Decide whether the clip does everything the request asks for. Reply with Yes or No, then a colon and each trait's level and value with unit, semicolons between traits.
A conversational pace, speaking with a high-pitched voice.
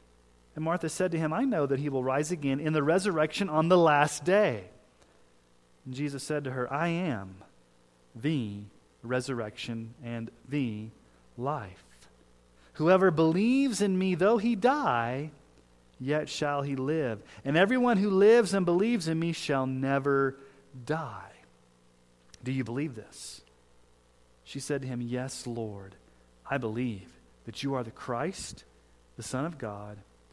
No: average, 145 wpm; low, 130 Hz